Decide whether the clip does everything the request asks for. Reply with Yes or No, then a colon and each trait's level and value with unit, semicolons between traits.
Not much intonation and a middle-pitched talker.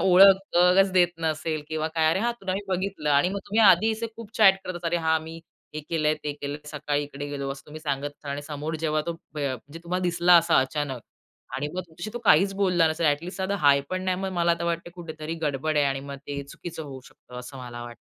No: average, 3.7 semitones; medium, 160 Hz